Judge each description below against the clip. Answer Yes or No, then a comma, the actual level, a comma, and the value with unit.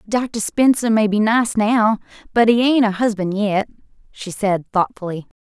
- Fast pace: No, average, 165 wpm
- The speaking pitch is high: Yes, high, 215 Hz